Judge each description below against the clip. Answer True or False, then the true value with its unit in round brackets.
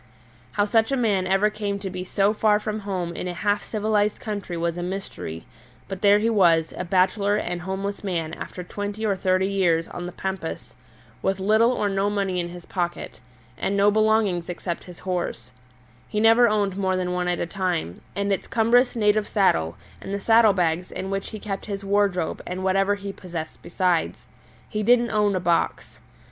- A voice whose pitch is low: False (195 Hz)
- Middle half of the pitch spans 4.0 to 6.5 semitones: False (2.6 semitones)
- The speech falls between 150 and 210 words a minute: True (195 wpm)